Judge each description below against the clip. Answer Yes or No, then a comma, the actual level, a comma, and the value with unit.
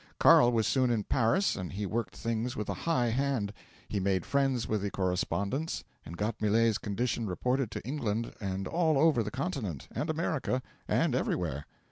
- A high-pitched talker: No, low, 115 Hz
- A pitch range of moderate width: Yes, average, 4.8 semitones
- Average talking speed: Yes, average, 175 wpm